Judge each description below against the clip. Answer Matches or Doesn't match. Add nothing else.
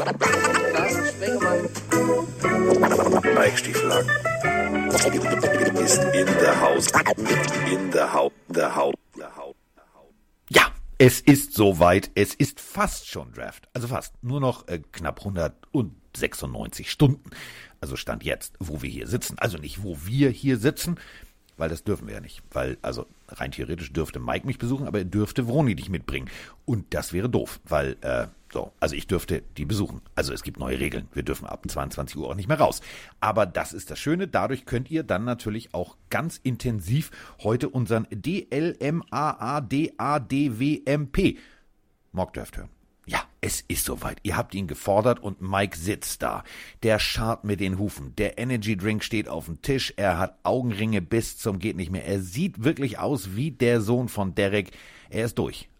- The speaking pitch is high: Doesn't match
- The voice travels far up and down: Matches